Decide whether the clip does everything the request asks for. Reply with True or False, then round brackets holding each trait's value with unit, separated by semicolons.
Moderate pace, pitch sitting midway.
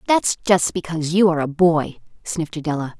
True (180 wpm; 170 Hz)